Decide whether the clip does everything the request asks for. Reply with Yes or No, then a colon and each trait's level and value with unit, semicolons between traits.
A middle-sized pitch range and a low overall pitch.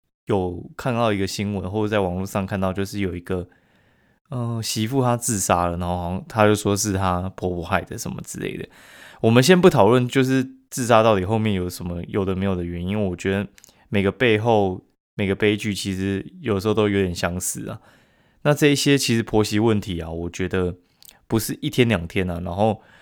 Yes: average, 3.5 semitones; low, 100 Hz